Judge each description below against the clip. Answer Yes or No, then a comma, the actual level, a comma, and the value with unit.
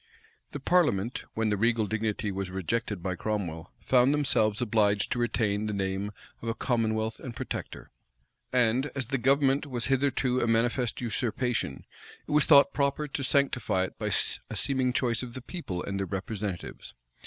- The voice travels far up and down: No, average, 4.2 semitones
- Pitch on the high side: No, low, 115 Hz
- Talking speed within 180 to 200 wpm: No, average, 165 wpm